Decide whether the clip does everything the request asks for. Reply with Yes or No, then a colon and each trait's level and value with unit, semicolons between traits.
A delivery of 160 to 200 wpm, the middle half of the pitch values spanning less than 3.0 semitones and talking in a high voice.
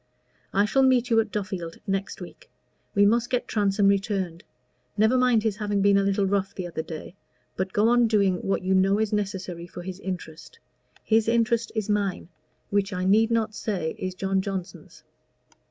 Yes: average, 185 wpm; narrow, 2.5 semitones; high, 200 Hz